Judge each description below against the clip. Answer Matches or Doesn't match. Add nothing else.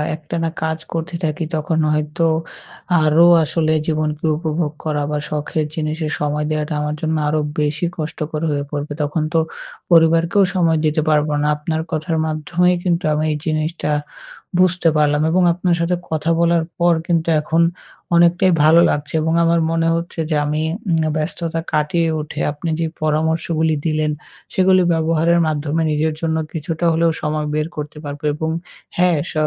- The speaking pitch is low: Doesn't match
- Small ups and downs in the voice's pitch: Matches